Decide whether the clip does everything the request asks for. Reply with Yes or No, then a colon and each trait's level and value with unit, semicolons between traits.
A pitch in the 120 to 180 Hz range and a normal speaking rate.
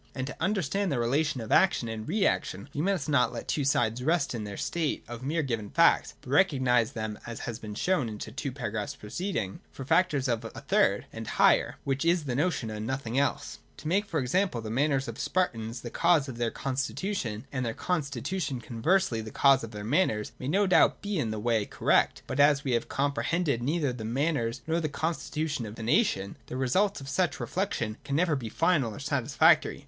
No: low, 135 Hz; fast, 220 wpm